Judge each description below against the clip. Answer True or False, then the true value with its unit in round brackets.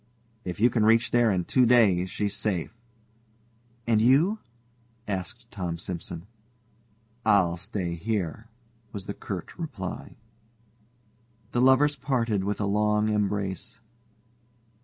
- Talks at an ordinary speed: False (115 wpm)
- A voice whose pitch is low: True (105 Hz)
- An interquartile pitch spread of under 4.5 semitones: True (3.9 semitones)